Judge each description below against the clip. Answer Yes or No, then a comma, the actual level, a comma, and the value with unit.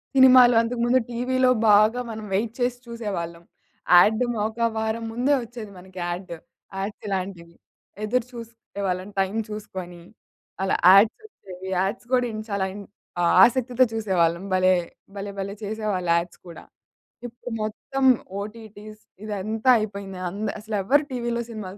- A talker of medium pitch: No, high, 215 Hz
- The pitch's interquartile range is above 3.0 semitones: Yes, average, 3.6 semitones